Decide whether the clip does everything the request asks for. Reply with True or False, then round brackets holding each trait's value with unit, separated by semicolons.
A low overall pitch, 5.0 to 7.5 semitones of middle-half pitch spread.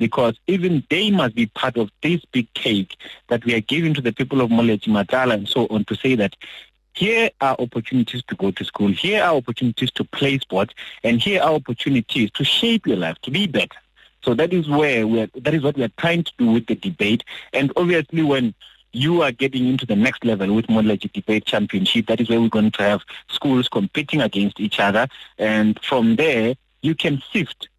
True (125 Hz; 5.5 semitones)